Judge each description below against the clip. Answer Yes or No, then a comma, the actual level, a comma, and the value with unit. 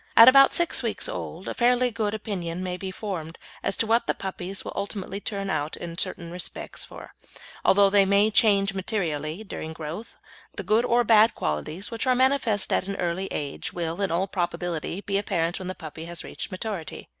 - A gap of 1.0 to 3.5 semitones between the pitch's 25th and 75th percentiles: No, average, 4.0 semitones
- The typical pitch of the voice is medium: No, high, 195 Hz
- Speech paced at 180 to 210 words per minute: Yes, average, 195 wpm